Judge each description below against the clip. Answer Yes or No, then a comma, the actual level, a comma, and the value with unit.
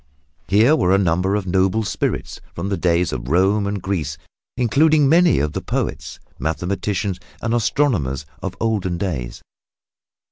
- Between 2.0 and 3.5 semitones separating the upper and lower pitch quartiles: No, average, 4.3 semitones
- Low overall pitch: Yes, very low, 95 Hz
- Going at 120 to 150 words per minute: Yes, average, 145 wpm